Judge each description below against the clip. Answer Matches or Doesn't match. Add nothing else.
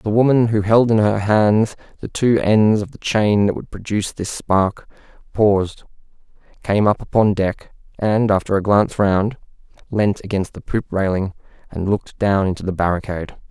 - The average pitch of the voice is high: Doesn't match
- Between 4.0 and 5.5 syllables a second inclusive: Matches